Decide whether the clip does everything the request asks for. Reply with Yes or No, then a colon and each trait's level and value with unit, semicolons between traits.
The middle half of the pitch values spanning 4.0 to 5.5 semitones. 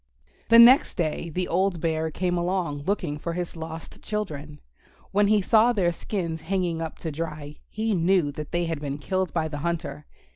No: average, 3.4 semitones